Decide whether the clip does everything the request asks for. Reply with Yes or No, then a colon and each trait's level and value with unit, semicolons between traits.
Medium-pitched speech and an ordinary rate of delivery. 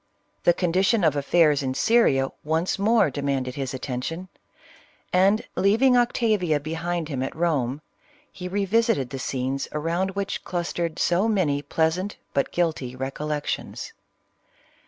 No: medium, 165 Hz; slow, 130 wpm